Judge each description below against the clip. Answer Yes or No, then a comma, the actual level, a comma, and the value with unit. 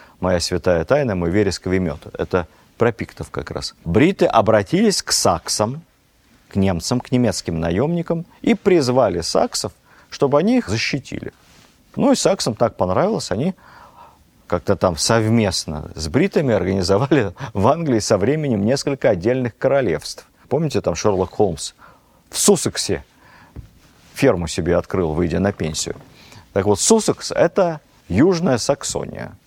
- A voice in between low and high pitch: No, low, 105 Hz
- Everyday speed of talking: Yes, average, 130 wpm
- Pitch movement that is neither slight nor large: No, wide, 7.3 semitones